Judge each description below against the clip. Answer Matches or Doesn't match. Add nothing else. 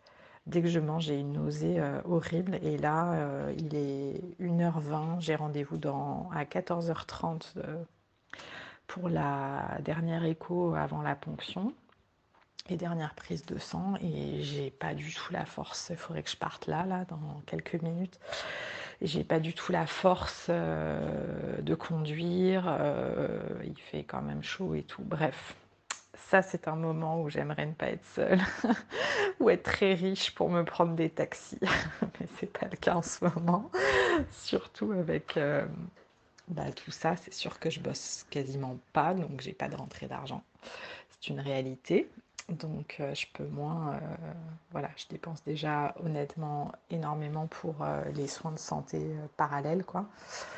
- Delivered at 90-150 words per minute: Doesn't match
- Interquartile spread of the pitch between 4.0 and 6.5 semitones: Doesn't match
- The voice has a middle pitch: Matches